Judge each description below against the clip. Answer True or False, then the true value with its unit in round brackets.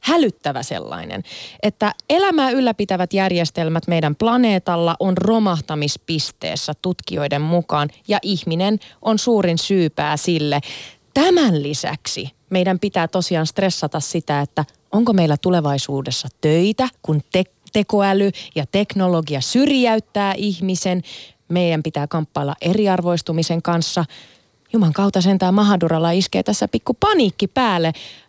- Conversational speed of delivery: True (110 wpm)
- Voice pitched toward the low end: False (180 Hz)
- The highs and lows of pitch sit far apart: False (4.5 semitones)